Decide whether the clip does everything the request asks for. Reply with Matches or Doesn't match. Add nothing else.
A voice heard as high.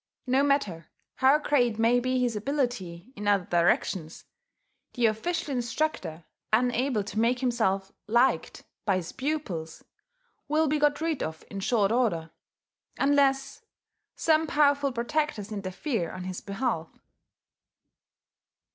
Matches